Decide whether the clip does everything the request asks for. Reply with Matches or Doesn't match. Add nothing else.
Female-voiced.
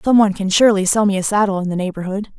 Matches